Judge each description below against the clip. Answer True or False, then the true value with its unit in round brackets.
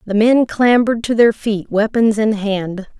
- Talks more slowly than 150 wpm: False (180 wpm)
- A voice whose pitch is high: True (215 Hz)